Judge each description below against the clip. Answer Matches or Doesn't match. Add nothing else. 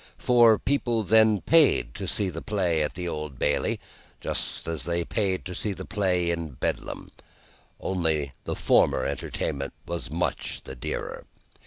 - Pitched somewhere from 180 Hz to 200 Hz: Doesn't match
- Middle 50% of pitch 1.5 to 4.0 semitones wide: Doesn't match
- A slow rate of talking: Doesn't match